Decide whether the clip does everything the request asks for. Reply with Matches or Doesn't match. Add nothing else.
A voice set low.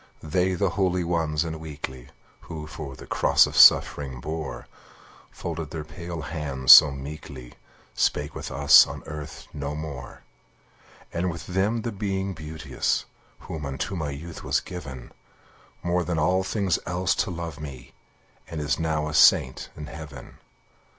Matches